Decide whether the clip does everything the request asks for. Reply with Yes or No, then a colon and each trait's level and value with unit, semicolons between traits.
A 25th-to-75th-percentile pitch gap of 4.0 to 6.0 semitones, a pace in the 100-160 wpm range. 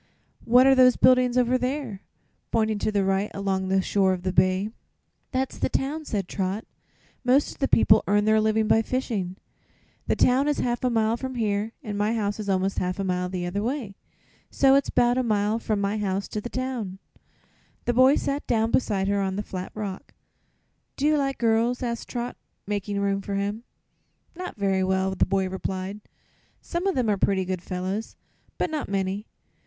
No: average, 4.3 semitones; average, 195 wpm